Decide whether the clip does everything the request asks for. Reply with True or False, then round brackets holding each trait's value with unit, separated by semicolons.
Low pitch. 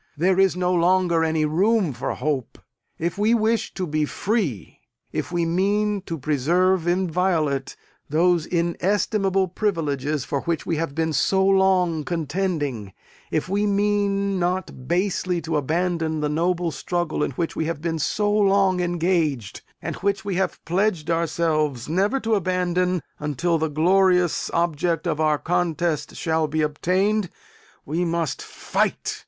False (175 Hz)